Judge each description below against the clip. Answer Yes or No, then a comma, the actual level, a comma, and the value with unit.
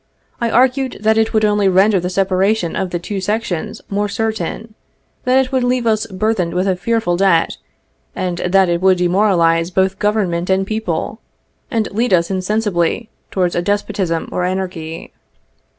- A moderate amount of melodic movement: Yes, average, 3.5 semitones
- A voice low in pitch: No, high, 195 Hz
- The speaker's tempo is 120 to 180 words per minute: Yes, average, 165 wpm